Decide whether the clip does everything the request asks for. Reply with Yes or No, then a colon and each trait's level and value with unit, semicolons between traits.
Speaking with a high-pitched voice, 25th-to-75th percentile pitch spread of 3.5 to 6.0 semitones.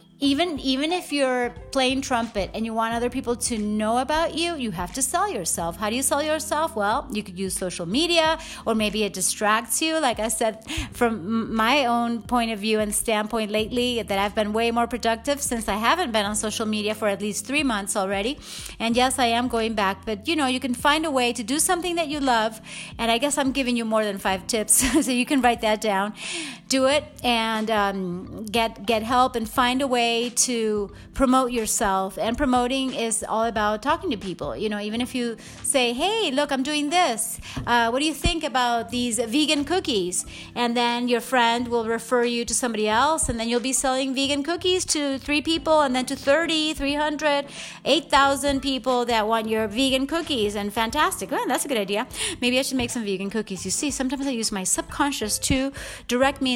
Yes: high, 245 Hz; average, 4.2 semitones